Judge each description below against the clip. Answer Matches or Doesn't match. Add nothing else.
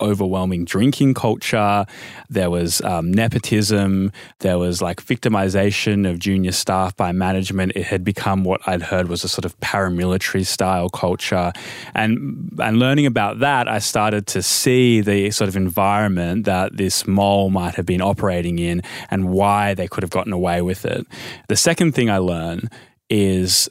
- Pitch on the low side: Matches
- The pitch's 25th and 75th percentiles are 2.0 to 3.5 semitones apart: Matches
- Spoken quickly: Doesn't match